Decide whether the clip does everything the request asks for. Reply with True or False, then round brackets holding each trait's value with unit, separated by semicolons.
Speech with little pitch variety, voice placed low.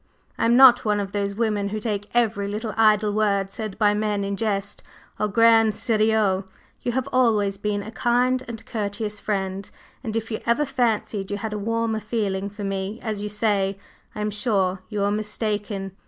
False (2.0 semitones; 210 Hz)